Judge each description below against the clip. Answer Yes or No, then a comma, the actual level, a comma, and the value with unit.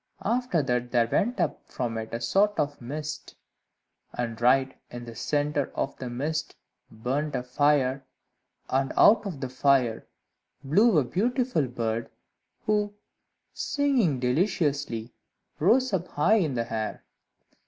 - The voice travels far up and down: Yes, wide, 6.9 semitones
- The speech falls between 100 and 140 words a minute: Yes, slow, 135 wpm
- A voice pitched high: No, medium, 140 Hz